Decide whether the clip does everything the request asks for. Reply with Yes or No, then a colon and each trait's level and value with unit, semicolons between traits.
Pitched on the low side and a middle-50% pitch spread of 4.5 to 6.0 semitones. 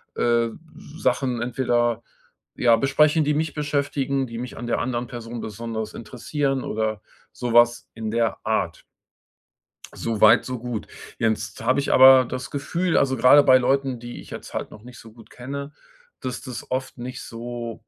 No: low, 125 Hz; average, 2.7 semitones